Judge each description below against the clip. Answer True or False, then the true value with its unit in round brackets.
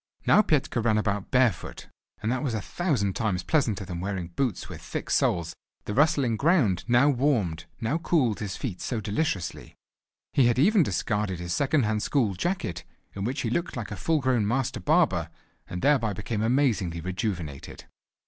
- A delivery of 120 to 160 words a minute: False (175 wpm)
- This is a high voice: False (115 Hz)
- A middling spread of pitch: False (6.2 semitones)